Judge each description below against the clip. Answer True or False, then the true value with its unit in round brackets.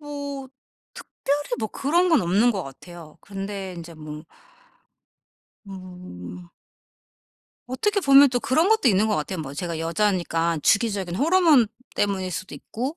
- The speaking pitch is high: True (200 Hz)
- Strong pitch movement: True (8.1 semitones)